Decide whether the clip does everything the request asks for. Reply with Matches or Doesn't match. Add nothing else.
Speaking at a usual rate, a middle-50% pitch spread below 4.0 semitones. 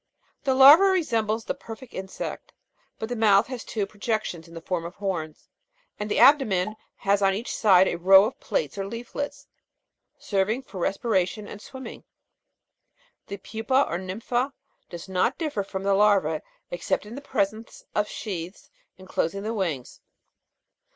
Matches